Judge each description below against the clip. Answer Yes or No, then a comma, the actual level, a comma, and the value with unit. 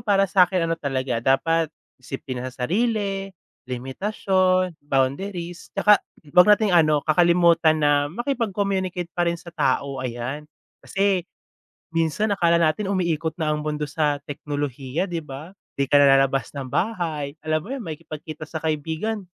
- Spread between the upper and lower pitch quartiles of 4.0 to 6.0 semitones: Yes, average, 4.5 semitones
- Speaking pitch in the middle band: Yes, medium, 165 Hz